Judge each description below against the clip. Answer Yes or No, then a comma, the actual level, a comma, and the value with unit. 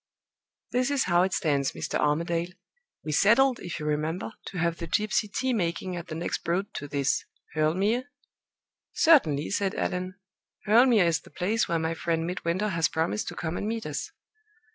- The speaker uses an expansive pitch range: No, average, 4.6 semitones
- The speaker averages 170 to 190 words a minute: Yes, average, 185 wpm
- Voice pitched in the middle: Yes, medium, 175 Hz